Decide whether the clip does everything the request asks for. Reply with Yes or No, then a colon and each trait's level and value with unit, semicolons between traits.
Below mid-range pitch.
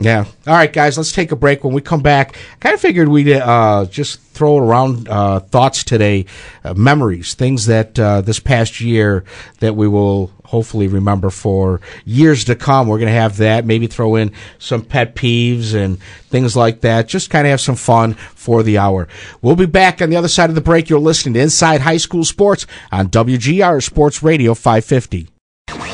Yes: low, 115 Hz